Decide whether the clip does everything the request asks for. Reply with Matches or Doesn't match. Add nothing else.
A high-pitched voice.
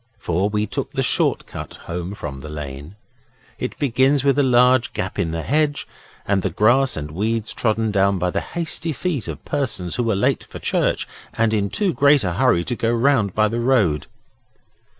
Doesn't match